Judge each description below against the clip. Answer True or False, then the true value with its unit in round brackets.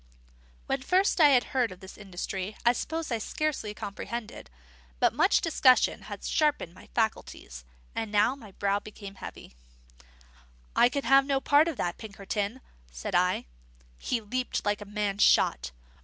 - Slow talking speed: False (155 wpm)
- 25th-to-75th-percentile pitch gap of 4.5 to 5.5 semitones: True (5.1 semitones)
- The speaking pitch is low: False (215 Hz)